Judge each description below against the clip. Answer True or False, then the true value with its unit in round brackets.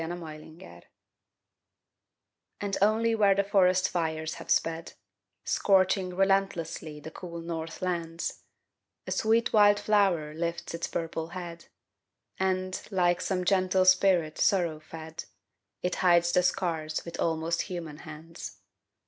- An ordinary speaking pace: False (125 wpm)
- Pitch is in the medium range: True (175 Hz)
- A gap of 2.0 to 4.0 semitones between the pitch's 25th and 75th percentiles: True (2.6 semitones)